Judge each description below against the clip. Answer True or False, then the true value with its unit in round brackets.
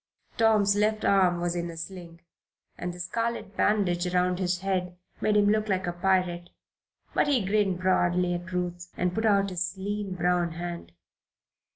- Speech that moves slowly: False (170 wpm)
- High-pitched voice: False (180 Hz)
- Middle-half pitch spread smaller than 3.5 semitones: True (2.4 semitones)